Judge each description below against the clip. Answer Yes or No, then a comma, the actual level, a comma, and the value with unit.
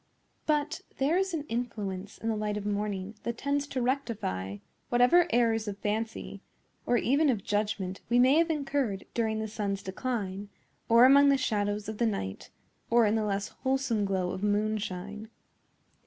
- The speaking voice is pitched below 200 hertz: No, high, 220 Hz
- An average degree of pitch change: Yes, average, 4.1 semitones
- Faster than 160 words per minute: Yes, average, 170 wpm